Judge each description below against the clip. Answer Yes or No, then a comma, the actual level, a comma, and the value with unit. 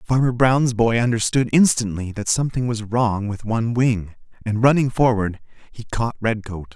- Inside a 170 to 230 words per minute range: No, average, 160 wpm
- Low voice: Yes, low, 115 Hz